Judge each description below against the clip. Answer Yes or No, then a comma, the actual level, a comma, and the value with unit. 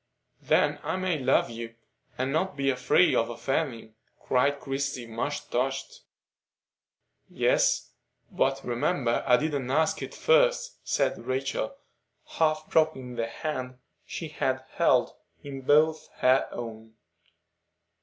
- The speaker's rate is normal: No, slow, 120 wpm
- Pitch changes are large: No, average, 3.8 semitones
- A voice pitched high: No, low, 135 Hz